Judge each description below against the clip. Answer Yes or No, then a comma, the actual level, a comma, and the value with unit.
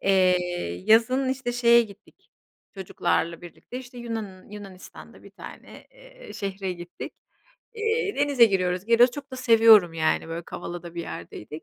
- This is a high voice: Yes, high, 205 Hz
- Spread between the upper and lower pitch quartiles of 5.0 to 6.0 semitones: Yes, wide, 5.5 semitones